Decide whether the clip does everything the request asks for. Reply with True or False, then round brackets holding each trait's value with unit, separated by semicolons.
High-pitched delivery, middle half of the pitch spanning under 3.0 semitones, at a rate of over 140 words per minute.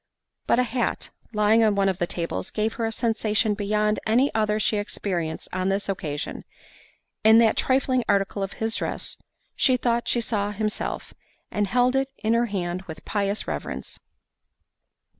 True (215 Hz; 2.6 semitones; 160 wpm)